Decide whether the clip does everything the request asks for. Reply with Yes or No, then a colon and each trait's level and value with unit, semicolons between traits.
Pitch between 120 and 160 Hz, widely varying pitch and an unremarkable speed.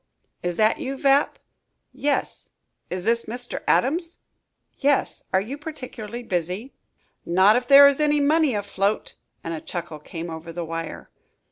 No: high, 225 Hz; wide, 7.9 semitones; average, 145 wpm